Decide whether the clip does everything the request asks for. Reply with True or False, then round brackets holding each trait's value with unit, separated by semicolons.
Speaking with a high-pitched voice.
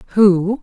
True (200 Hz)